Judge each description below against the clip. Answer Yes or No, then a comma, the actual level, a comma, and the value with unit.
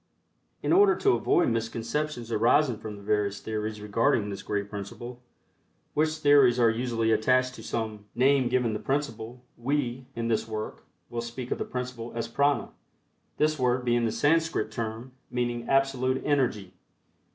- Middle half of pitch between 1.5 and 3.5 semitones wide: Yes, average, 3.0 semitones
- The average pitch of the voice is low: Yes, low, 120 Hz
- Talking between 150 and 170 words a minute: Yes, average, 155 wpm